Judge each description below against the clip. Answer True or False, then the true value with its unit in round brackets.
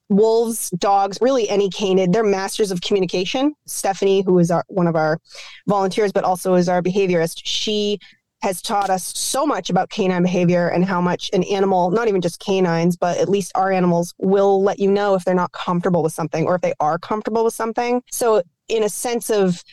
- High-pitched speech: True (195 Hz)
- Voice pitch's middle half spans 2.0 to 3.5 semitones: True (2.6 semitones)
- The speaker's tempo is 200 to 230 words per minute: True (205 wpm)